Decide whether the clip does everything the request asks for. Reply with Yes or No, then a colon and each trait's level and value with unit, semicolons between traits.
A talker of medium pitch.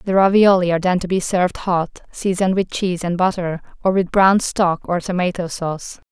Yes: medium, 180 Hz